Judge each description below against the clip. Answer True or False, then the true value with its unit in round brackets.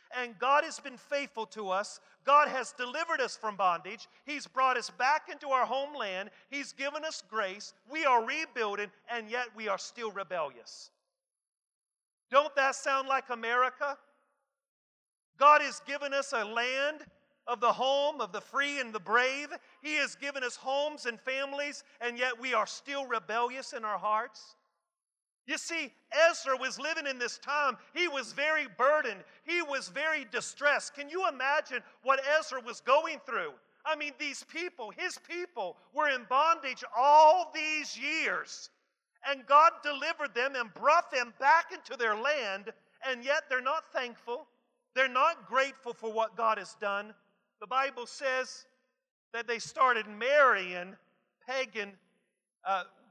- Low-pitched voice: False (265 Hz)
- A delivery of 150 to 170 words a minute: True (155 wpm)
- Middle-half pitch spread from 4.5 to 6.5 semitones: False (3.8 semitones)